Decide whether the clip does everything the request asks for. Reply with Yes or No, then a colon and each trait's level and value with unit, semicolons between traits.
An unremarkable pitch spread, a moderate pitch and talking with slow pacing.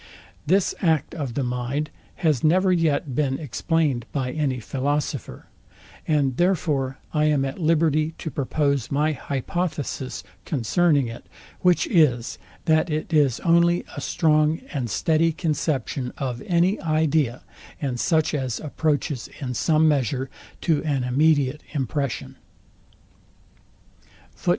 Yes: average, 3.3 semitones; medium, 150 Hz; slow, 120 wpm